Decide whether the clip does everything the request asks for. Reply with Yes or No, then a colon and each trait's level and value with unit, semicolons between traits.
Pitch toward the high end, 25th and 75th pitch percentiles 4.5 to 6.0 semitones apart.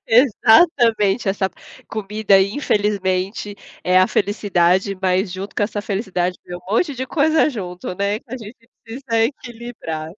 No: high, 205 Hz; average, 3.6 semitones